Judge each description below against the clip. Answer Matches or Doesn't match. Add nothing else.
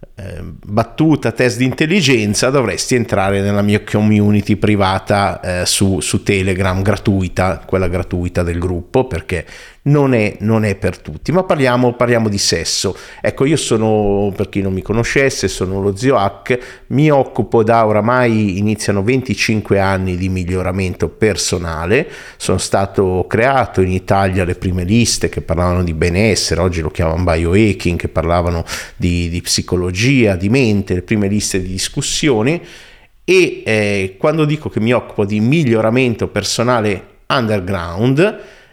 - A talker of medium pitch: Doesn't match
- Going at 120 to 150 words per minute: Matches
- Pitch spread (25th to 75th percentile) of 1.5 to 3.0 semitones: Doesn't match